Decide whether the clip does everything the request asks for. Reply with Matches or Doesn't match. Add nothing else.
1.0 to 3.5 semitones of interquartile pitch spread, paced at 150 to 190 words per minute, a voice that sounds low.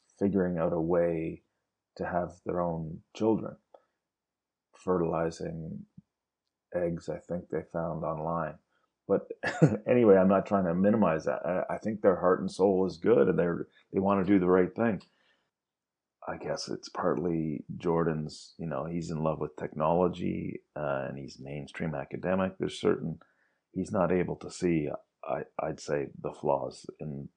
Matches